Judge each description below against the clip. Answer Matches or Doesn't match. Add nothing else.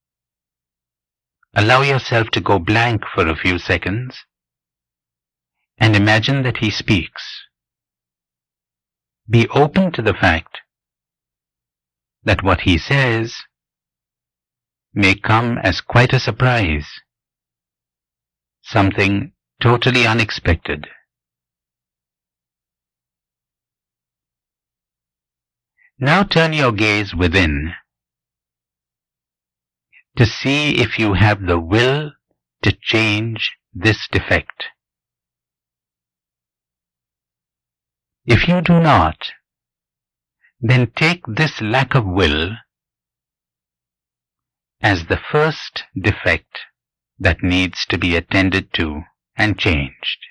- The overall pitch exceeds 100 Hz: Doesn't match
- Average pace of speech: Doesn't match